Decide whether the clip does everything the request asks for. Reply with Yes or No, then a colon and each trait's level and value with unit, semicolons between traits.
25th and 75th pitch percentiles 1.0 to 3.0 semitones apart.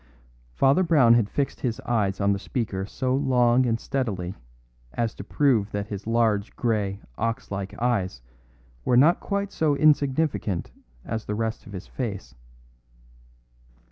No: average, 4.7 semitones